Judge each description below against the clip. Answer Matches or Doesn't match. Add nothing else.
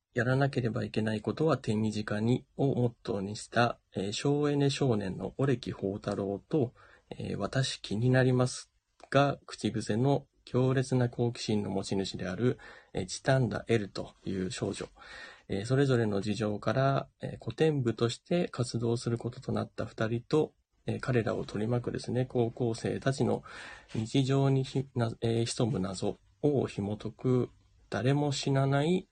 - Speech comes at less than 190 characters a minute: Doesn't match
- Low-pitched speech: Matches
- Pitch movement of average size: Matches